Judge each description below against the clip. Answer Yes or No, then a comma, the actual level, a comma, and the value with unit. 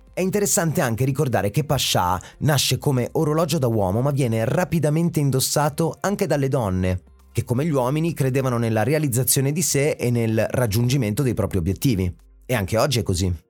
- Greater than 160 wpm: Yes, fast, 170 wpm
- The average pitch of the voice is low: Yes, low, 130 Hz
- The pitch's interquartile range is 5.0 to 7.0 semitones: Yes, average, 5.3 semitones